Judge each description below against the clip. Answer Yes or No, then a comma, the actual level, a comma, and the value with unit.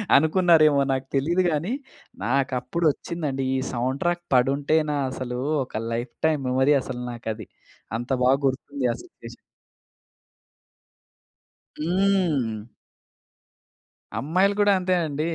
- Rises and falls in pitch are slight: No, average, 4.7 semitones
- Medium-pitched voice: Yes, medium, 145 Hz